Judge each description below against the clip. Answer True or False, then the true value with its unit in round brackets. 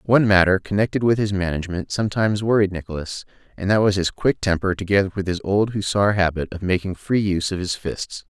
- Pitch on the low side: True (95 Hz)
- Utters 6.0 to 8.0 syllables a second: True (6.2 syllables/s)